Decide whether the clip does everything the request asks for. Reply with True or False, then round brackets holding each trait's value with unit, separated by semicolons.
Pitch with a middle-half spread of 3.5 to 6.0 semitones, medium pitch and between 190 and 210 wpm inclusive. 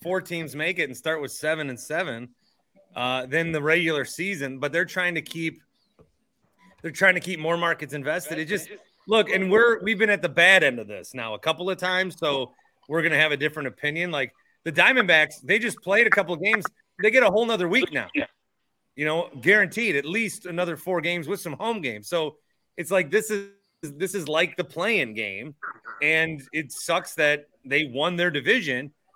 True (3.9 semitones; 170 Hz; 205 wpm)